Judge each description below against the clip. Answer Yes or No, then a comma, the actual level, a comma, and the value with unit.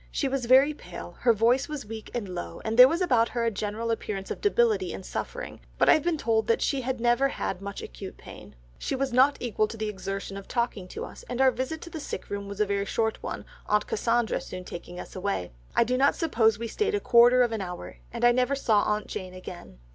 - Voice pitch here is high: Yes, high, 230 Hz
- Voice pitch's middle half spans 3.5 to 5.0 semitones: Yes, average, 4.4 semitones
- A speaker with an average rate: No, fast, 245 wpm